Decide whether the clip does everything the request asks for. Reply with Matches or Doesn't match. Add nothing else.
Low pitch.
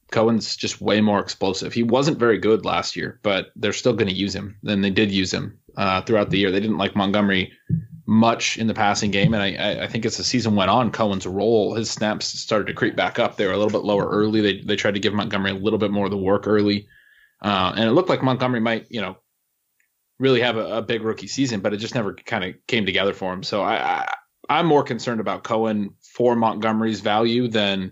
Matches